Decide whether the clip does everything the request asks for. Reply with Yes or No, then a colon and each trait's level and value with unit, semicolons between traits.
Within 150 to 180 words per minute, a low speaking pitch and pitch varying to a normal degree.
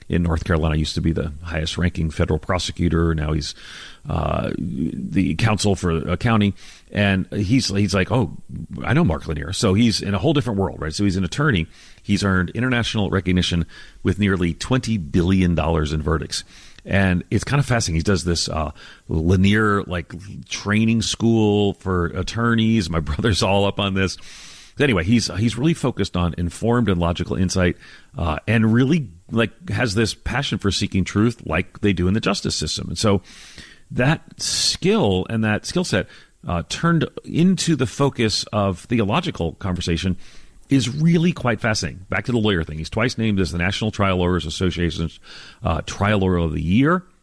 Yes: average, 175 wpm; very low, 95 Hz; average, 4.4 semitones